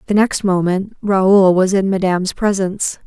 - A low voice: No, high, 190 Hz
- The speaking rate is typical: Yes, average, 155 wpm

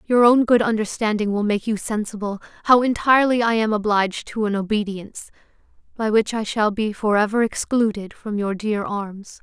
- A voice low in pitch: No, high, 215 Hz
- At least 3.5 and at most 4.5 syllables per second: No, 5.2 syllables/s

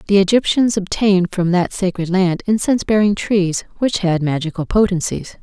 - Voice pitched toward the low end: No, high, 190 Hz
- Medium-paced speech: Yes, average, 155 wpm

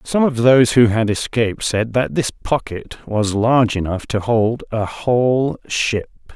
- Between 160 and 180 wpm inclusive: Yes, average, 170 wpm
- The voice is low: Yes, low, 115 Hz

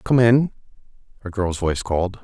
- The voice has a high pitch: No, low, 105 Hz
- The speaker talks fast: No, average, 160 wpm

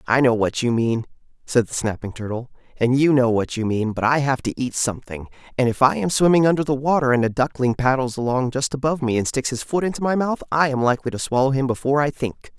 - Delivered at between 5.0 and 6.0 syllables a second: No, 6.2 syllables/s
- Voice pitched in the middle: No, low, 130 Hz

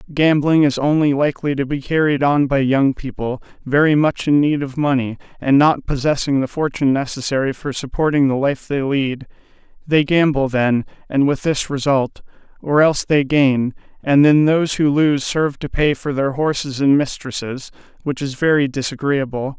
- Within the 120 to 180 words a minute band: Yes, average, 175 wpm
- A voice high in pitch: No, medium, 140 Hz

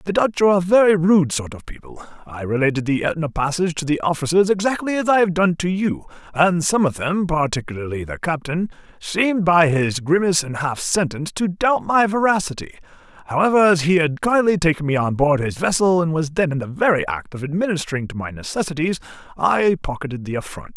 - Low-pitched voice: No, medium, 165 Hz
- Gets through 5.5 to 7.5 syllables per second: Yes, 5.9 syllables/s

